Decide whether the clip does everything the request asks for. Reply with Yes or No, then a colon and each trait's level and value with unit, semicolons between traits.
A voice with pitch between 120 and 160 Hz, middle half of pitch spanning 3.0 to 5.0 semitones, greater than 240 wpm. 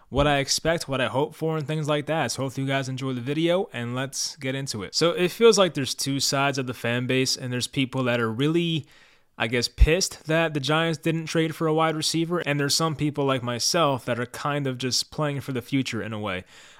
Yes: medium, 140 Hz; average, 3.7 semitones; fast, 250 wpm